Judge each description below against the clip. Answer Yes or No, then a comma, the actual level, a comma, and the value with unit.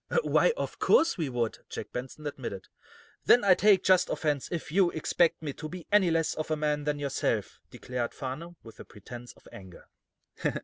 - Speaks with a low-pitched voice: No, medium, 155 Hz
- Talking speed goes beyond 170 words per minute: Yes, average, 185 wpm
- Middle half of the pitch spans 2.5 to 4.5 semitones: No, average, 5.2 semitones